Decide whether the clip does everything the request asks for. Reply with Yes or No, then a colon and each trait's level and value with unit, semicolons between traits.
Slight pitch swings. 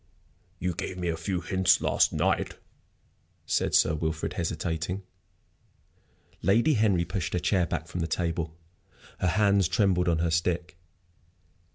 Yes: narrow, 2.3 semitones